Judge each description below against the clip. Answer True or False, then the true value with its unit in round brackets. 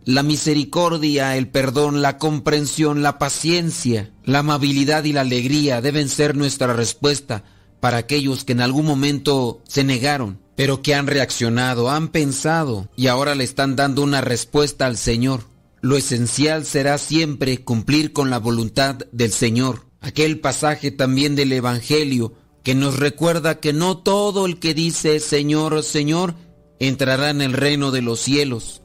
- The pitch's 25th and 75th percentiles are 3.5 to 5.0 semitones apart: False (2.8 semitones)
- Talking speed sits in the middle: True (150 wpm)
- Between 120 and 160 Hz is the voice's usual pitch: True (140 Hz)